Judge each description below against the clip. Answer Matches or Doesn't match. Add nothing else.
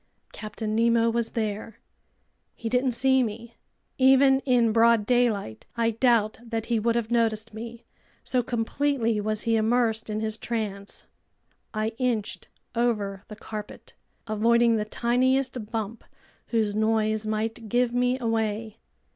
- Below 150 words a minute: Matches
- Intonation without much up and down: Matches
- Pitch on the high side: Matches